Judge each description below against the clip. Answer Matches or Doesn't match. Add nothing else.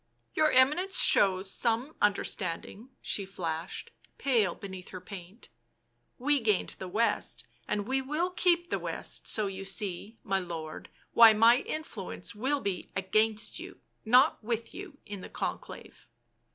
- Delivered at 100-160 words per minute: Matches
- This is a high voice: Matches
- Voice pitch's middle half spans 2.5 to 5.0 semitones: Doesn't match